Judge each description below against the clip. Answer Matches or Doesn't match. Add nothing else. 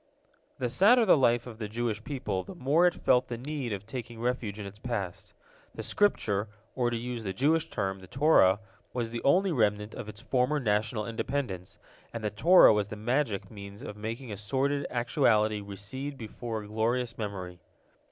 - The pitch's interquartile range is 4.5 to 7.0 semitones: Doesn't match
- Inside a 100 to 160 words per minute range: Doesn't match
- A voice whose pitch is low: Matches